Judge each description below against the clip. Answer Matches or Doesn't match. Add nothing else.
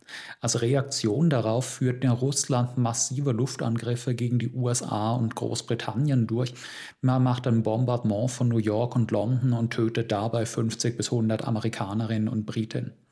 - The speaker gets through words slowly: Doesn't match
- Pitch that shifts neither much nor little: Doesn't match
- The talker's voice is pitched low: Matches